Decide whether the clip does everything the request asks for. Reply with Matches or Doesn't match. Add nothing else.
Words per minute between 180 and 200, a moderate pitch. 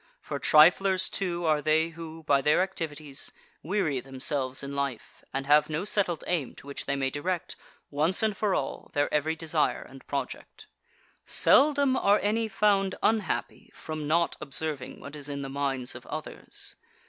Doesn't match